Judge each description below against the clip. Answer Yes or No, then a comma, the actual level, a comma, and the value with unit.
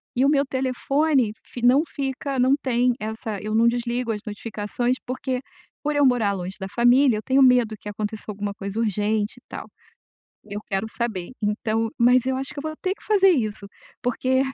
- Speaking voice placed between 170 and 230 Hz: No, high, 240 Hz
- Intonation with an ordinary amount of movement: Yes, average, 3.7 semitones